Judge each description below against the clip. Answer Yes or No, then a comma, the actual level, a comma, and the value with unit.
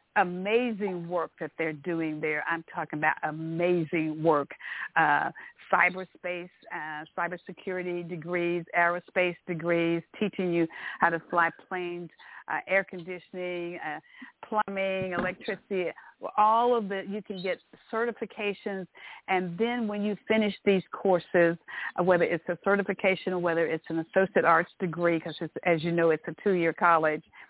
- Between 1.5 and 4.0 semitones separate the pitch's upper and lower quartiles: Yes, narrow, 2.4 semitones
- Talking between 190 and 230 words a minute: No, average, 140 wpm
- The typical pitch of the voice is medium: Yes, medium, 180 Hz